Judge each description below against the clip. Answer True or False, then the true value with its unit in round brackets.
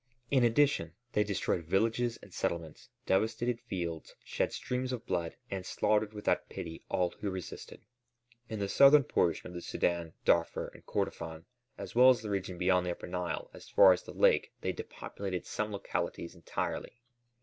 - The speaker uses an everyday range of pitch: True (4.6 semitones)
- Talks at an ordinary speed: True (170 wpm)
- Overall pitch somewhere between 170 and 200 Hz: False (95 Hz)